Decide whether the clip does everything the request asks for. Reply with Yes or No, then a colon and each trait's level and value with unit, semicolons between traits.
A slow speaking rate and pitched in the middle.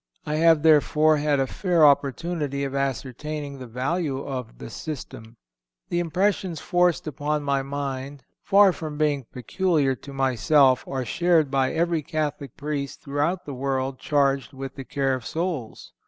No: average, 155 wpm; medium, 145 Hz